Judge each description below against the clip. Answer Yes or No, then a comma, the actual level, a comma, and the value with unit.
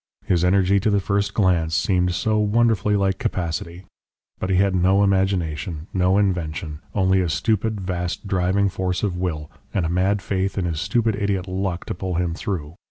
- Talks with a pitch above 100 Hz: No, very low, 95 Hz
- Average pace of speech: Yes, average, 180 wpm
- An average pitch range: No, narrow, 2.2 semitones